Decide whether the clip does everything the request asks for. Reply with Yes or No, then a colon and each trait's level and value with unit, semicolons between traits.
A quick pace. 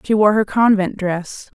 No: average, 190 wpm